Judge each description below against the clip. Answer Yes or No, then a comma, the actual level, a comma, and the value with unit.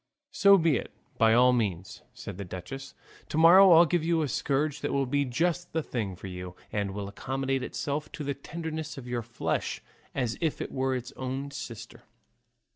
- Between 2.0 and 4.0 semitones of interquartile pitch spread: No, average, 5.0 semitones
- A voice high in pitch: No, low, 135 Hz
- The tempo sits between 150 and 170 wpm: No, average, 195 wpm